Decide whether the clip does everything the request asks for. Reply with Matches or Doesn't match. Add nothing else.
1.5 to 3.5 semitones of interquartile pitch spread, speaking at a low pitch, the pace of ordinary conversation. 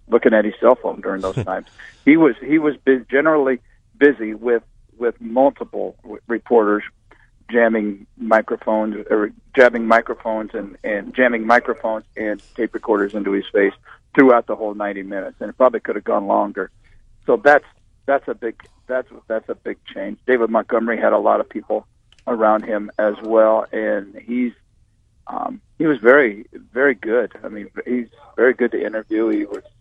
Matches